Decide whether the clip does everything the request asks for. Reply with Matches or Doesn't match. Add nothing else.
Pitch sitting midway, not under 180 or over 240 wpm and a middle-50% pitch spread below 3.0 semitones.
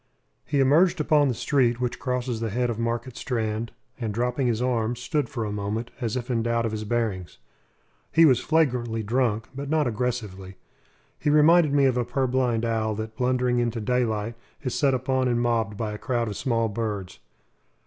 Doesn't match